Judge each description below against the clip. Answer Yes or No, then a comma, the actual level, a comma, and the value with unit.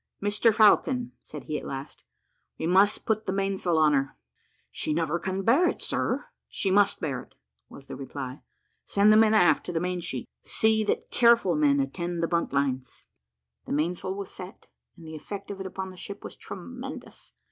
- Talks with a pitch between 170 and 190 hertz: Yes, medium, 185 Hz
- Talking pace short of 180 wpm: No, average, 185 wpm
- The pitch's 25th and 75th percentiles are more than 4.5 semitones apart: Yes, average, 5.1 semitones